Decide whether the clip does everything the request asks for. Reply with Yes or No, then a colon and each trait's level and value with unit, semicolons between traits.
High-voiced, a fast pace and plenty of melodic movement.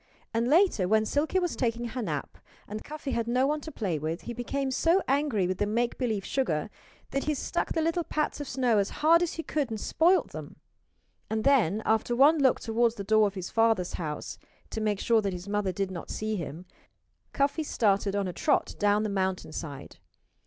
Yes: high, 225 Hz; fast, 210 wpm; wide, 5.9 semitones